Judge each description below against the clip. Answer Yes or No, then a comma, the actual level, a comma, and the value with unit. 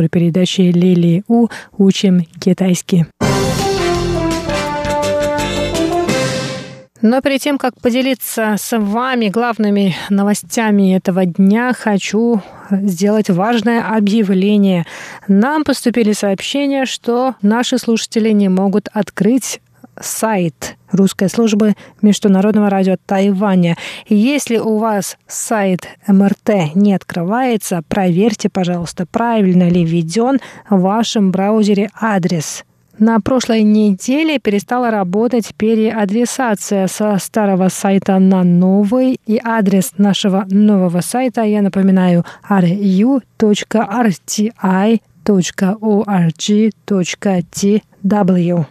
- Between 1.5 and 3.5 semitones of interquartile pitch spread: Yes, average, 3.1 semitones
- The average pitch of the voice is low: No, high, 205 Hz